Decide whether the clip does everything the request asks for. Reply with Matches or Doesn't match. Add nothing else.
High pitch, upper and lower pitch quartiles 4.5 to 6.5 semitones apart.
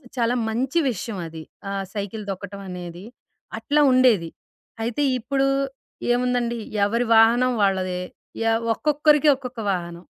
Matches